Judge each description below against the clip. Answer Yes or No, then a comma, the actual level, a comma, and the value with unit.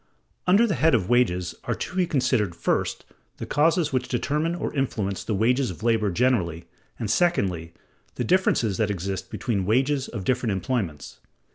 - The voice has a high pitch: No, low, 115 Hz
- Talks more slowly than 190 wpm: Yes, average, 170 wpm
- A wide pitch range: Yes, wide, 6.5 semitones